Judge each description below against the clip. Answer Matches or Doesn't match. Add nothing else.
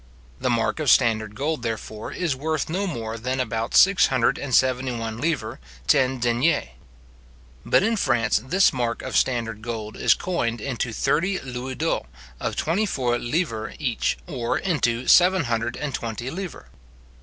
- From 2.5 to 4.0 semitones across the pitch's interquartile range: Doesn't match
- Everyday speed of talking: Matches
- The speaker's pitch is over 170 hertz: Doesn't match